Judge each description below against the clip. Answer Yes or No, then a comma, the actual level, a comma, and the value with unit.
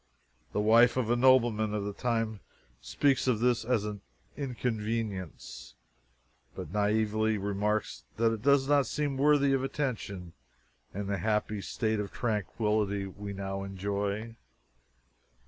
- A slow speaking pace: Yes, slow, 130 wpm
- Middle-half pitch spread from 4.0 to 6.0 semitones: No, average, 3.2 semitones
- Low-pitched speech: Yes, low, 110 Hz